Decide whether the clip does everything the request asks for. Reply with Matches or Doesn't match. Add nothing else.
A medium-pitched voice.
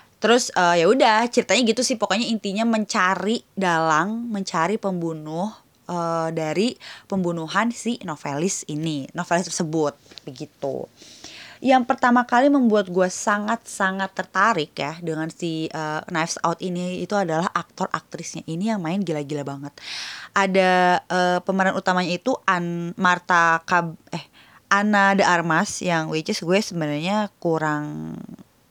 Matches